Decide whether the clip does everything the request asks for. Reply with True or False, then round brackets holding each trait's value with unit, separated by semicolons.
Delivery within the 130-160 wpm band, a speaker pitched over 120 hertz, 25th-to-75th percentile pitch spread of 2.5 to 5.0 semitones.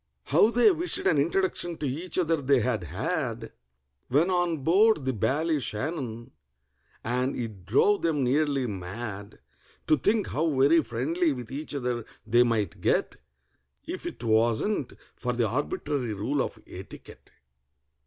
False (140 wpm; 135 Hz; 5.6 semitones)